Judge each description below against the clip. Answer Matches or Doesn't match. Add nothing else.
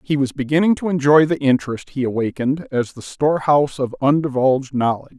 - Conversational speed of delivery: Matches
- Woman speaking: Doesn't match